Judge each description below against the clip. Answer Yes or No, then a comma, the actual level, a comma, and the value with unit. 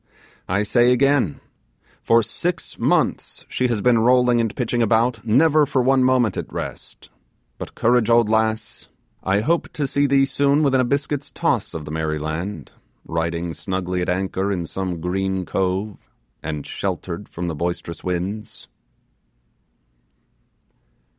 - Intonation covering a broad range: Yes, wide, 5.7 semitones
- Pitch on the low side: Yes, low, 110 Hz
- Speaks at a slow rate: No, average, 145 wpm